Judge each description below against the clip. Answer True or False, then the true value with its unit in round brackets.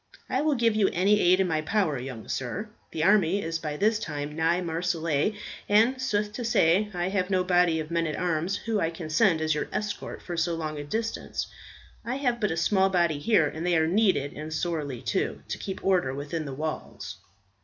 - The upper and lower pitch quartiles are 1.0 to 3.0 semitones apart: False (4.6 semitones)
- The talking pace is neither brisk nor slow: False (215 wpm)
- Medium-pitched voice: True (175 Hz)